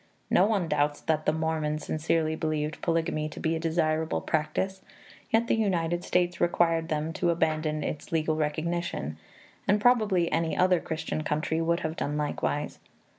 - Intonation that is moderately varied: No, narrow, 2.0 semitones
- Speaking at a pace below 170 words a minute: Yes, average, 160 wpm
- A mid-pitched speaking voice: Yes, medium, 160 Hz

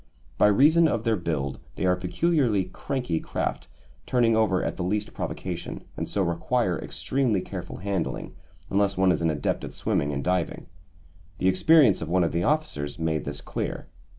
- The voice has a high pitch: No, very low, 95 Hz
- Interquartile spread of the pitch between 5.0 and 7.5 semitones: Yes, average, 5.3 semitones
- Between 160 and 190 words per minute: Yes, average, 175 wpm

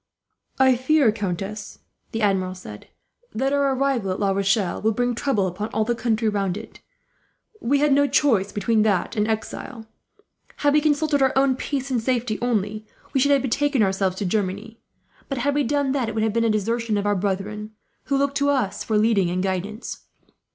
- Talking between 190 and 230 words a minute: Yes, average, 195 wpm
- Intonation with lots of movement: No, average, 4.8 semitones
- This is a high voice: Yes, high, 225 Hz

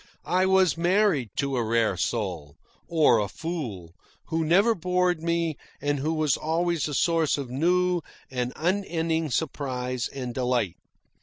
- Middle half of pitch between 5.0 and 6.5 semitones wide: Yes, wide, 5.5 semitones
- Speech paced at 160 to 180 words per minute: No, average, 145 wpm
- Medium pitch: Yes, medium, 155 Hz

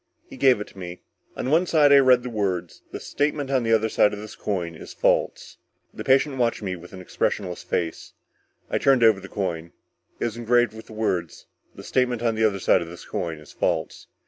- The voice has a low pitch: Yes, low, 110 Hz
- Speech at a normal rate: No, fast, 225 wpm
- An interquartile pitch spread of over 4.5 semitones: Yes, wide, 5.4 semitones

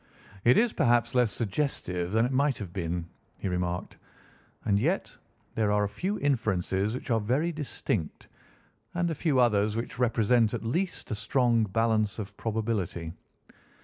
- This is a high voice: No, low, 115 Hz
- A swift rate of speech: No, average, 155 wpm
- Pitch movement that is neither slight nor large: Yes, average, 3.8 semitones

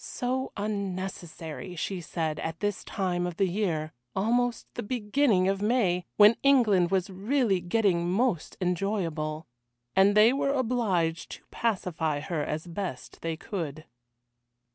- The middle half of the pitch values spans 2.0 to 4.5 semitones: Yes, average, 4.2 semitones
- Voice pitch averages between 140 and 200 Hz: Yes, high, 190 Hz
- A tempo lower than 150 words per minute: Yes, slow, 135 wpm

